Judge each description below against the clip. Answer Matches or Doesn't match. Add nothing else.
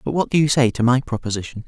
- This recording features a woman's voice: Doesn't match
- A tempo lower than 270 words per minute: Doesn't match